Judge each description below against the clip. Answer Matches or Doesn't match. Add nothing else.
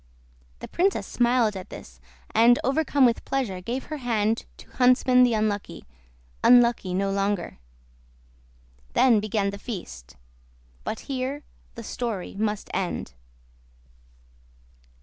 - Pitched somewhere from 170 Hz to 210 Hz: Doesn't match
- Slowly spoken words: Matches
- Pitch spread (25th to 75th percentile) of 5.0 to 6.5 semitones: Doesn't match